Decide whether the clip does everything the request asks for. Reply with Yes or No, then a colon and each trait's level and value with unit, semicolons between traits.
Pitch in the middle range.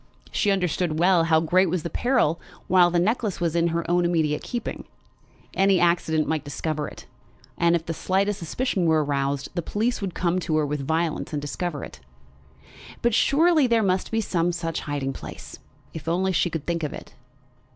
Yes: medium, 170 Hz